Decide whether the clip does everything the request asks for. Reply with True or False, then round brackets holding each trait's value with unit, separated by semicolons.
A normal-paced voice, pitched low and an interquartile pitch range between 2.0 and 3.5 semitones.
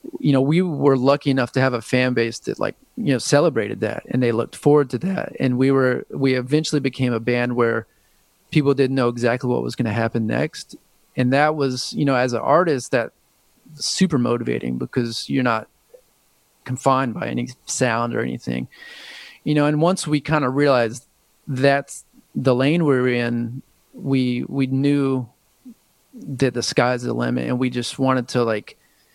True (185 wpm; 130 Hz; 2.9 semitones)